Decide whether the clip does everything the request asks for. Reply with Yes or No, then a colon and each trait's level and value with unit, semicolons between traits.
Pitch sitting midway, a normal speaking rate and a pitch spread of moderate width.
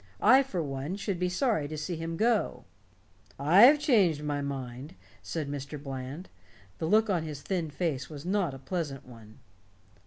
Yes: medium, 155 Hz; average, 165 wpm; average, 4.9 semitones